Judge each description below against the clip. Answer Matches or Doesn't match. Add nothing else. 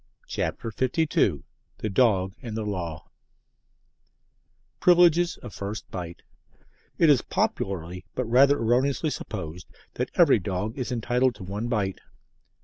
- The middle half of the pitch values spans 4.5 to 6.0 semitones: Matches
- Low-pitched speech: Matches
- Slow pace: Matches